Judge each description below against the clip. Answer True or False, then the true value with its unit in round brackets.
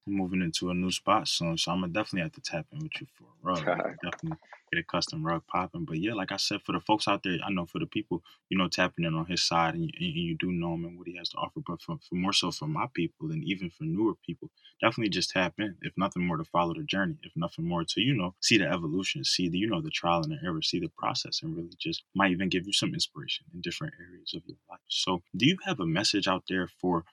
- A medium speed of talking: False (290 wpm)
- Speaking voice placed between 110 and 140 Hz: False (100 Hz)